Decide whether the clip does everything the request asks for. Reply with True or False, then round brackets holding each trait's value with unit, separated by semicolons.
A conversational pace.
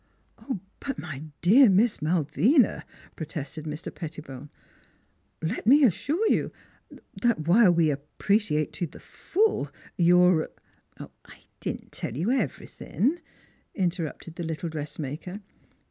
False (125 wpm)